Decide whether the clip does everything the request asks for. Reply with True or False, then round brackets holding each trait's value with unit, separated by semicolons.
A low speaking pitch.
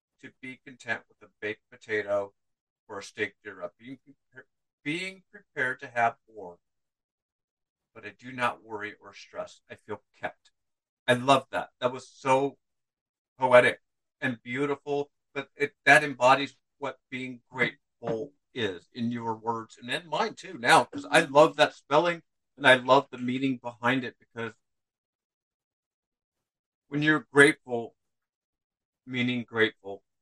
True (125 Hz)